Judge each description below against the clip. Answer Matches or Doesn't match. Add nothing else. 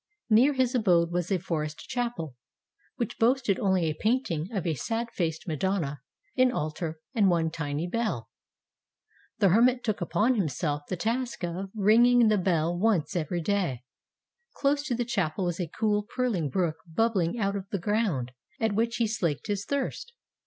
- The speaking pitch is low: Doesn't match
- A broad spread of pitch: Matches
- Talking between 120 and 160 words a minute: Doesn't match